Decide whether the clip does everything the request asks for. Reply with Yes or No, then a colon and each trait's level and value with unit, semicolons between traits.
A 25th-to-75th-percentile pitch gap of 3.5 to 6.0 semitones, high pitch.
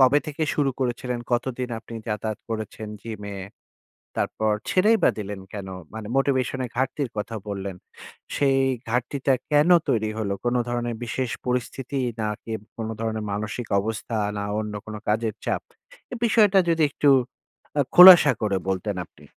No: average, 3.9 semitones; low, 115 Hz